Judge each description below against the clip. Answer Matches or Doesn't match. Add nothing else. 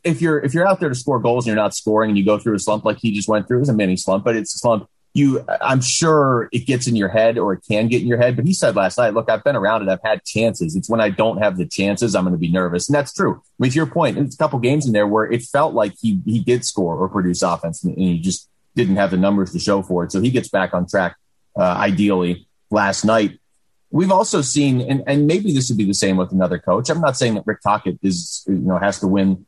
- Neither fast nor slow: Doesn't match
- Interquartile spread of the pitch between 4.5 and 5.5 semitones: Matches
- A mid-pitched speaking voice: Doesn't match